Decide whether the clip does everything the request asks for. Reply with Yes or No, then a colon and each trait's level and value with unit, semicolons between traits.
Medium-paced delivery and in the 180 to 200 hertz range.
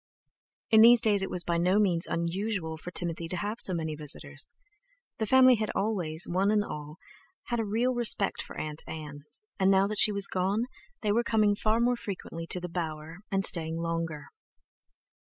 Yes: average, 190 wpm; medium, 185 Hz